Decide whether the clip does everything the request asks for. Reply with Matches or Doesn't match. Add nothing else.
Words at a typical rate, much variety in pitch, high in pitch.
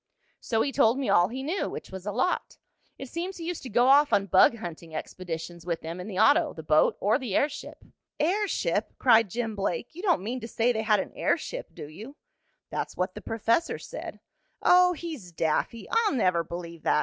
Doesn't match